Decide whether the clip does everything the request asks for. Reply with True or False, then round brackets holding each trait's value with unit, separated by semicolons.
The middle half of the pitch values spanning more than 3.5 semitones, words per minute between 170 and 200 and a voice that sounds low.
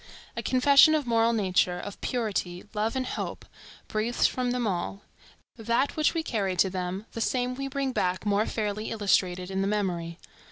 False (4.7 semitones; 175 wpm; 215 Hz)